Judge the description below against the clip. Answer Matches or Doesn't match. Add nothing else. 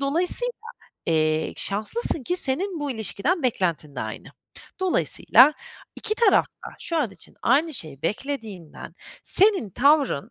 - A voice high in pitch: Matches